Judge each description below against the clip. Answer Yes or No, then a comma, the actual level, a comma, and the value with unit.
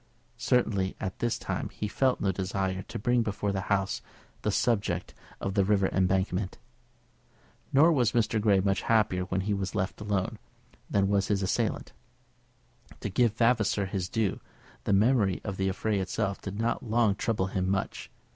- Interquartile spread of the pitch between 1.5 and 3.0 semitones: Yes, narrow, 2.6 semitones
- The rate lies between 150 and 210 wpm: Yes, average, 170 wpm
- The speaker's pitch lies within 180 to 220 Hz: No, low, 100 Hz